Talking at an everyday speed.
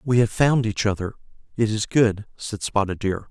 Yes: average, 180 wpm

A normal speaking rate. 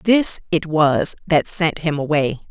Yes: average, 170 wpm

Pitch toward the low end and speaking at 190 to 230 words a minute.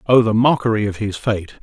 Yes: low, 110 Hz; fast, 220 wpm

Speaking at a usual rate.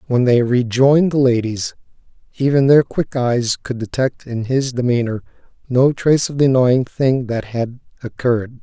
Yes: average, 160 wpm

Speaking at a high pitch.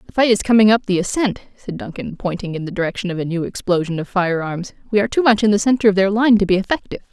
Yes: high, 195 Hz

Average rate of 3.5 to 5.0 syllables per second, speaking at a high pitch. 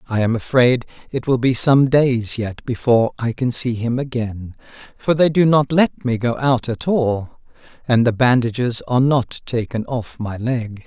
No: 4.5 syllables/s; low, 120 Hz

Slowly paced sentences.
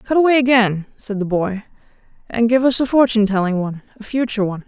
No: fast, 205 wpm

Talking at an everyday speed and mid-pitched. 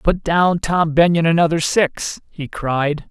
Yes: average, 155 wpm; medium, 165 Hz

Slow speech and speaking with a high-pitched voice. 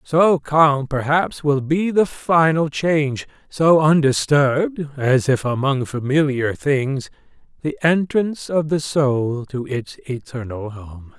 No: slow, 125 wpm; medium, 145 Hz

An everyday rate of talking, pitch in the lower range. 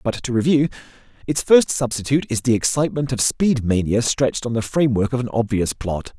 Yes: average, 195 wpm; low, 120 Hz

